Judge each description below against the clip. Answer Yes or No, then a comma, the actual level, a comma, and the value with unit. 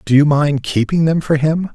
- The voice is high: No, medium, 150 Hz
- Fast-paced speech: Yes, fast, 240 wpm